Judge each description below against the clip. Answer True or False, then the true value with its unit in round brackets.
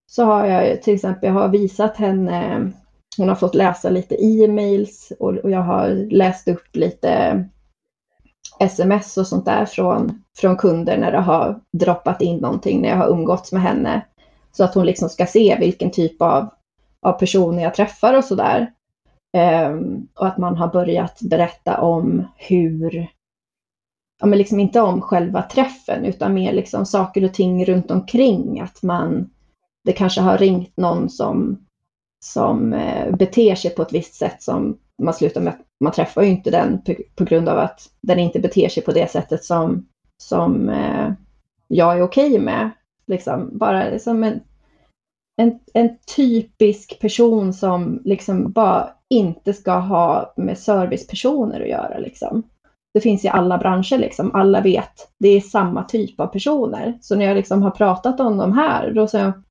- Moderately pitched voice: False (195 Hz)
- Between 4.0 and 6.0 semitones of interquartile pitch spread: False (3.2 semitones)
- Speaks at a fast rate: False (170 wpm)